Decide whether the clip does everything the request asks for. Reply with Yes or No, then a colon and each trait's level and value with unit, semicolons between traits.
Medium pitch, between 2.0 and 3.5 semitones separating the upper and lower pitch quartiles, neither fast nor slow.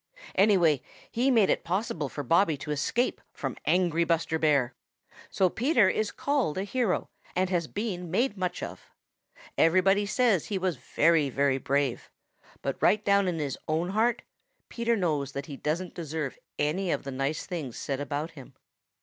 No: medium, 170 Hz; average, 5.2 semitones; average, 170 wpm